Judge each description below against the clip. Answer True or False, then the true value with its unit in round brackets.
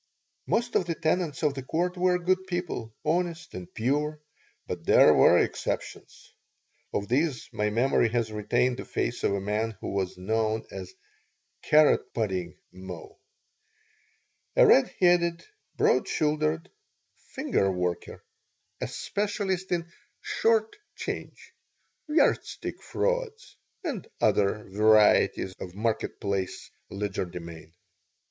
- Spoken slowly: True (120 wpm)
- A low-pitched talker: True (130 Hz)